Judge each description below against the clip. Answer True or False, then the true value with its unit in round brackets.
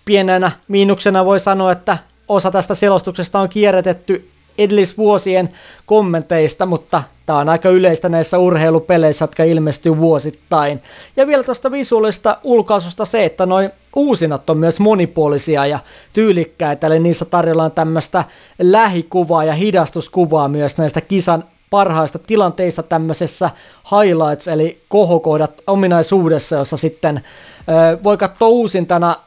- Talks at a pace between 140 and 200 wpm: False (120 wpm)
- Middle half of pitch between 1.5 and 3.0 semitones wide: False (3.6 semitones)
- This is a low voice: False (175 Hz)